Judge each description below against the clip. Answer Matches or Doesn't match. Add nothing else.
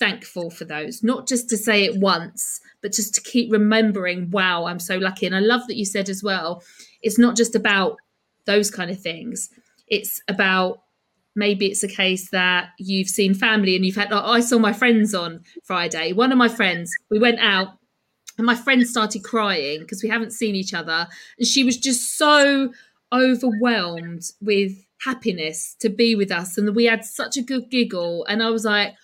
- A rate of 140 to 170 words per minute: Doesn't match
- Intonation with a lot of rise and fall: Doesn't match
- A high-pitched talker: Matches